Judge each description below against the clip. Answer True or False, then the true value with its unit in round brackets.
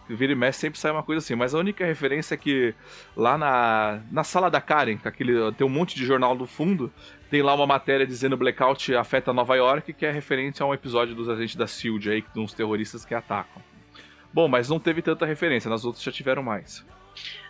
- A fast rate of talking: True (215 wpm)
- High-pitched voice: False (130 Hz)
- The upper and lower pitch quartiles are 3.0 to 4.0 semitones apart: False (4.6 semitones)